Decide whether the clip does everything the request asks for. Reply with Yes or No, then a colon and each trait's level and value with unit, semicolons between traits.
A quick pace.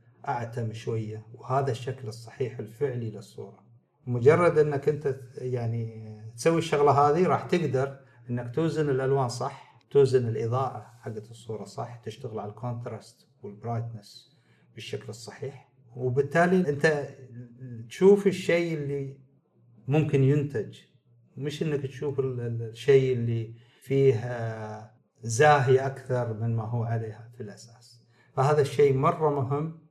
No: average, 110 wpm